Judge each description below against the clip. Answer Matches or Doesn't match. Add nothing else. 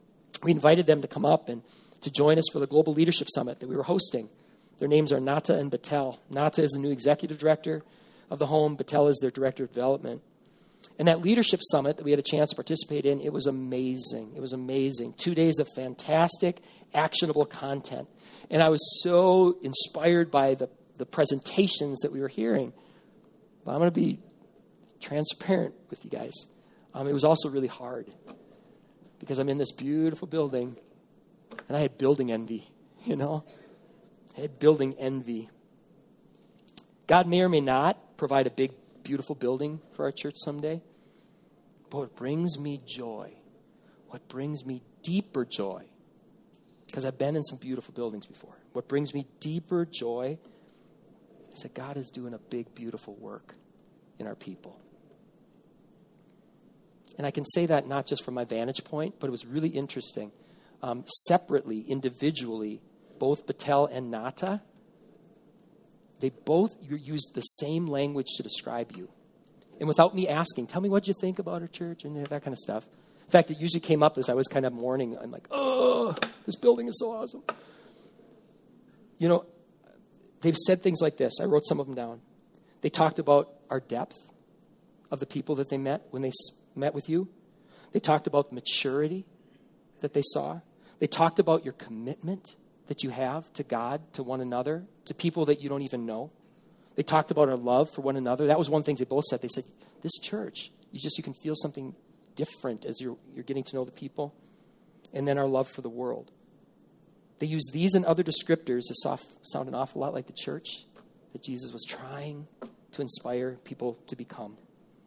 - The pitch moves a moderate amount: Matches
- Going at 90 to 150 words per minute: Doesn't match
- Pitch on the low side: Doesn't match